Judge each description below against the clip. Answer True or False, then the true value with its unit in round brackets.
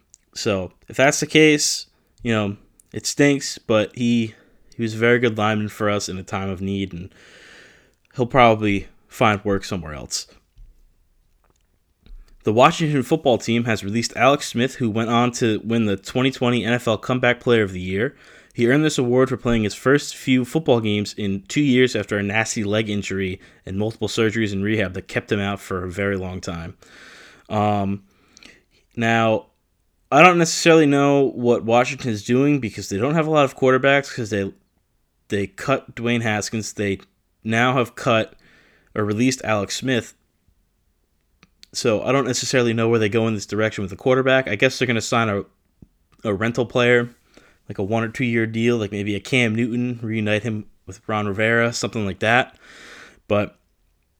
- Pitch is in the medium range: False (110 Hz)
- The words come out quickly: False (180 wpm)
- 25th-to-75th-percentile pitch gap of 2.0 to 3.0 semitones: False (3.7 semitones)